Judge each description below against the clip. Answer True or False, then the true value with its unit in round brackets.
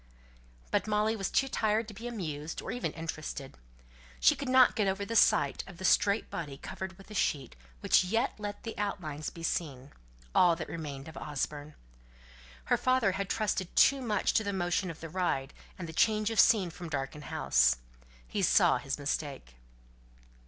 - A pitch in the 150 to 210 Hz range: True (185 Hz)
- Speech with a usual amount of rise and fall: False (5.8 semitones)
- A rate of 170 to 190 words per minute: True (185 wpm)